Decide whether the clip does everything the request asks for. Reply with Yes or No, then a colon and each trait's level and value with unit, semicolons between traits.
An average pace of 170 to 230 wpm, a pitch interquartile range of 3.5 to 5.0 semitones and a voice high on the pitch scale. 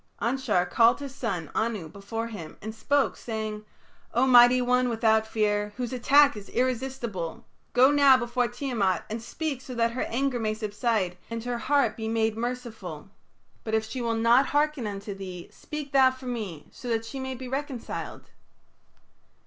No: average, 175 wpm; average, 3.0 semitones; high, 235 Hz